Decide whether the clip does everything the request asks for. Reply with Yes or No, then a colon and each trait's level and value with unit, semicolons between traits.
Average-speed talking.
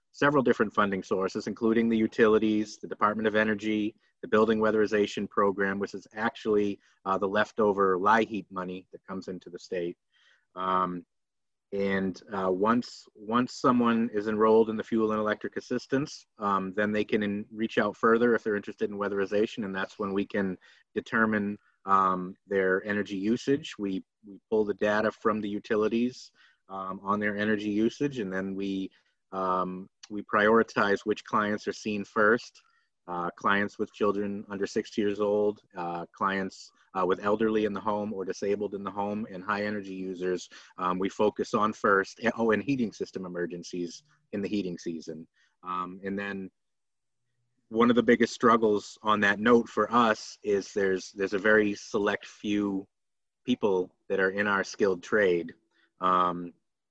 Yes: average, 165 wpm